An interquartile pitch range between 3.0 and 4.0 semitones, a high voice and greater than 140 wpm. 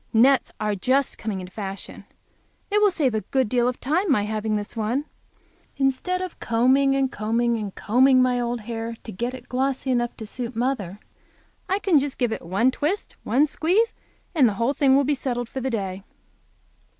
Yes: average, 3.7 semitones; very high, 250 Hz; average, 200 wpm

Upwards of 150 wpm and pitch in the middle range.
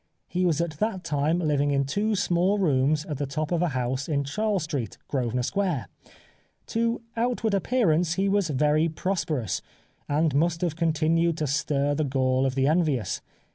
Yes: average, 175 wpm; medium, 155 Hz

